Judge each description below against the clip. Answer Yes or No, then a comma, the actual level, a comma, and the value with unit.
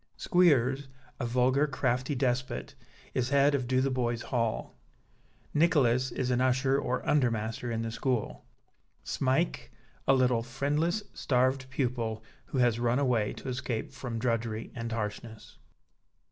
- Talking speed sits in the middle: No, slow, 130 wpm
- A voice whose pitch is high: No, low, 125 Hz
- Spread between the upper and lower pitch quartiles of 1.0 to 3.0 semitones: Yes, narrow, 2.4 semitones